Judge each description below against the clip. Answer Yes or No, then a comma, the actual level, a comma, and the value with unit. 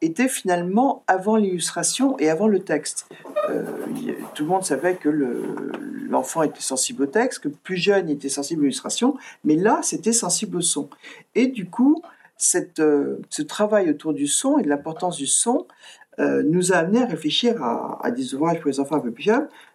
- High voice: Yes, high, 195 Hz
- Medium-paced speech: Yes, average, 195 wpm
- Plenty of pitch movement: Yes, wide, 8.9 semitones